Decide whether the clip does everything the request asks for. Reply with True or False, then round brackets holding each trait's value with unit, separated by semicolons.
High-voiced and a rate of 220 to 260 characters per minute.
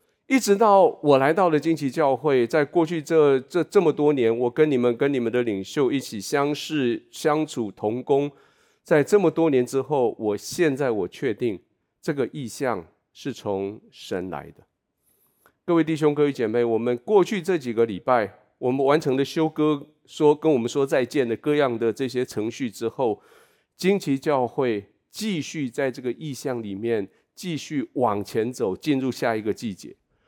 False (140 Hz; 250 characters per minute)